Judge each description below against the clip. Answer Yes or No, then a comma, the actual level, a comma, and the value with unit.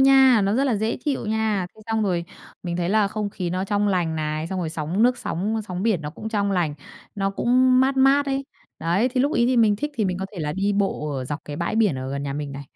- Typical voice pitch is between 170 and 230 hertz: Yes, high, 200 Hz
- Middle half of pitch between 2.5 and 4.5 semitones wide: No, average, 5.2 semitones